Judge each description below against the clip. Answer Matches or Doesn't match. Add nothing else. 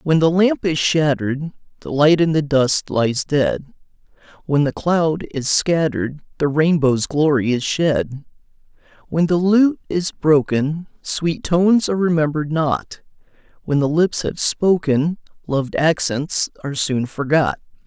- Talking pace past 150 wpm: Doesn't match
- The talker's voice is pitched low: Doesn't match